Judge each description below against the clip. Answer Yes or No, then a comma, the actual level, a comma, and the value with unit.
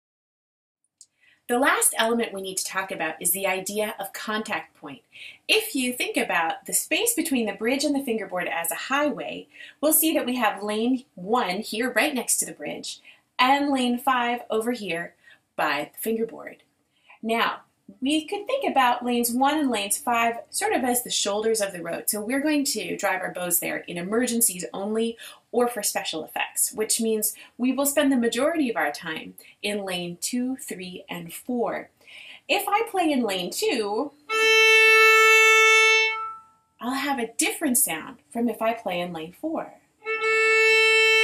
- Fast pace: No, average, 170 wpm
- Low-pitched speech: No, high, 245 Hz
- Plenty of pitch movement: Yes, wide, 6.5 semitones